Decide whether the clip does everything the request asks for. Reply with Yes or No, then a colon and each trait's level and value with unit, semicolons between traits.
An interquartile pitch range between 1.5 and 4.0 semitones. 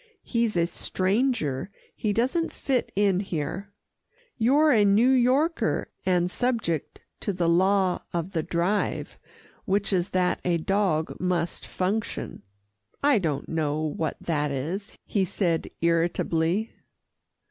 No: average, 4.5 semitones